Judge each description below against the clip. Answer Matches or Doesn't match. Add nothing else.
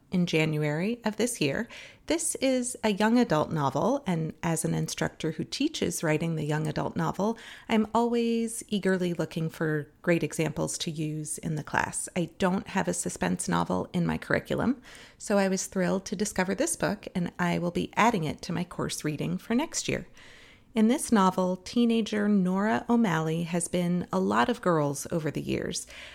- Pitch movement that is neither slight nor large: Doesn't match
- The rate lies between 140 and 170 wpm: Doesn't match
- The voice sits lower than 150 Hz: Doesn't match